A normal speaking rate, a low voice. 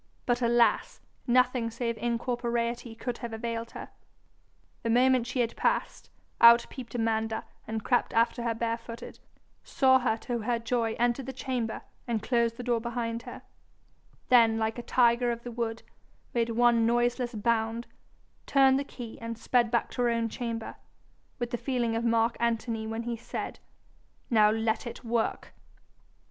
No: average, 160 wpm; high, 235 Hz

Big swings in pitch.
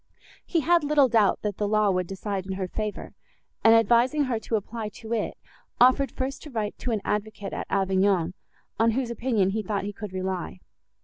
No: average, 3.4 semitones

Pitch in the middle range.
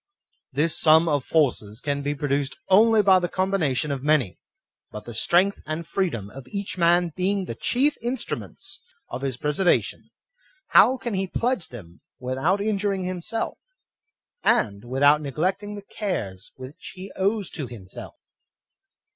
Yes: medium, 160 Hz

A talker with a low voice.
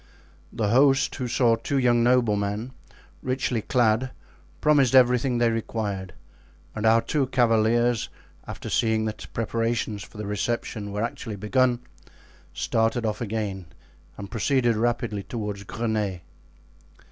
Yes: low, 115 Hz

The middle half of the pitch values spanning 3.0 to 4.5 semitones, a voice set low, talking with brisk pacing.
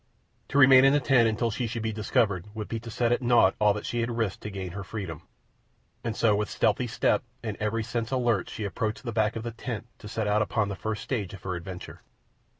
No: narrow, 2.4 semitones; low, 110 Hz; fast, 245 wpm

